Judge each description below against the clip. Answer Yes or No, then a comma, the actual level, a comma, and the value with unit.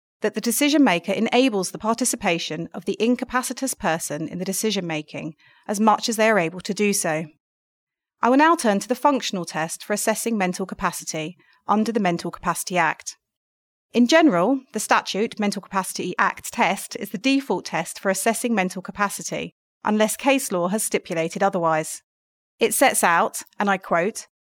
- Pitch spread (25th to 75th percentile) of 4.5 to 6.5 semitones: Yes, average, 5.1 semitones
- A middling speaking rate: Yes, average, 170 wpm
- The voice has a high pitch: Yes, high, 205 Hz